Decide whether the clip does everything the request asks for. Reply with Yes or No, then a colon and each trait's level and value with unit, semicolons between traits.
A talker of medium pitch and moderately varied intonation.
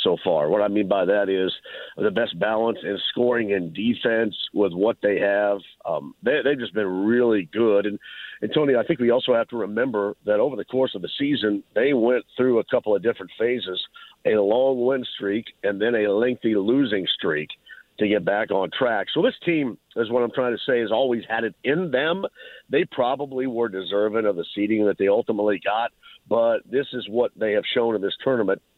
No: low, 115 Hz; average, 3.9 semitones